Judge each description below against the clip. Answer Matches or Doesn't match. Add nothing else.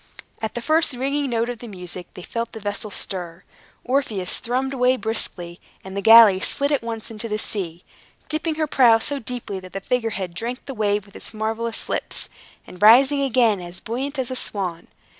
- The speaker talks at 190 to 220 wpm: Matches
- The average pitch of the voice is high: Matches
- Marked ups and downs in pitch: Doesn't match